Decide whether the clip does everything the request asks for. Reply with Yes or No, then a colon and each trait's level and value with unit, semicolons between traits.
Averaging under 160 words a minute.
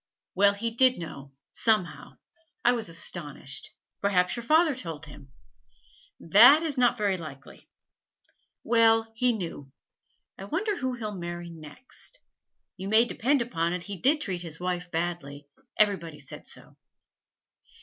Yes: average, 140 wpm